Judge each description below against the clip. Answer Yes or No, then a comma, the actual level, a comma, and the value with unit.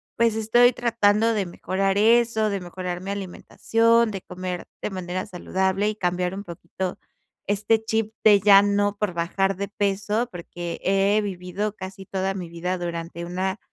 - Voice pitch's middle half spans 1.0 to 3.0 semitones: Yes, narrow, 2.6 semitones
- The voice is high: Yes, high, 195 Hz